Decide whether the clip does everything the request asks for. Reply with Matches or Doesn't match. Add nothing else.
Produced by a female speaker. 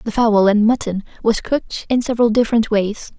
Matches